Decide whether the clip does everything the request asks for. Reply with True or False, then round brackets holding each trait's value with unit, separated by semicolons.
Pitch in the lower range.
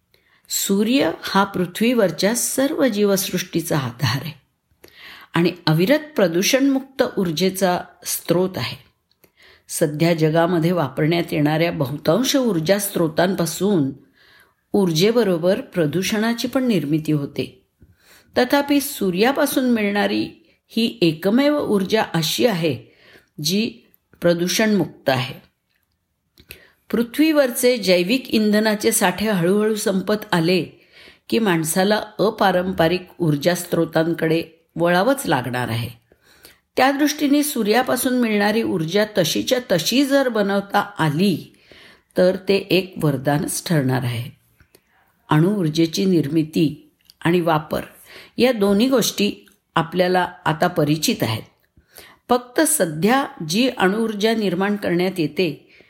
False (185 Hz)